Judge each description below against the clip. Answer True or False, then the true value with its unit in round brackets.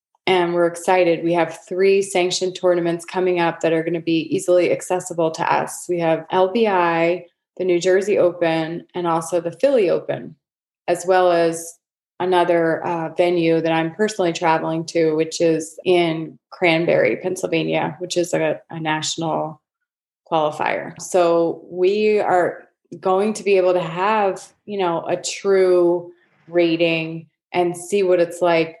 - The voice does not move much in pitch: True (1.8 semitones)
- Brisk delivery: False (150 wpm)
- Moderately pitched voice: True (175 Hz)